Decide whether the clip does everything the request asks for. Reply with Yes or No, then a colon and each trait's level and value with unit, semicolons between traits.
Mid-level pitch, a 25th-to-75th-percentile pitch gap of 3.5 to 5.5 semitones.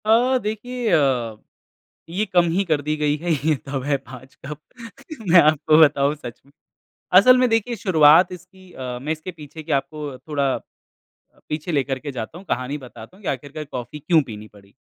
Yes: medium, 150 Hz; average, 4.9 semitones